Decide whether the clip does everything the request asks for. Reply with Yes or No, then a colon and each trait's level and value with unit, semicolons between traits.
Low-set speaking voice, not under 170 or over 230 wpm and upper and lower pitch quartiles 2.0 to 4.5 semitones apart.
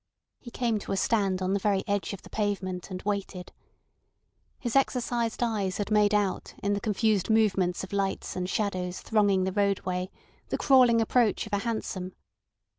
No: high, 200 Hz; average, 175 wpm; average, 2.7 semitones